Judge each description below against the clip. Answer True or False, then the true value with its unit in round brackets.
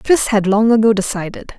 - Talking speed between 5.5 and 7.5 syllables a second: True (5.6 syllables/s)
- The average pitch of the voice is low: False (215 Hz)